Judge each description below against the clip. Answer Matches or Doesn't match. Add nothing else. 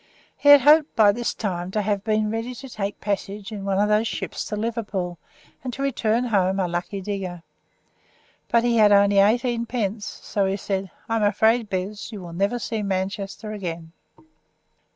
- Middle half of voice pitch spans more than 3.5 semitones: Doesn't match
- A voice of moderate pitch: Doesn't match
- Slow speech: Doesn't match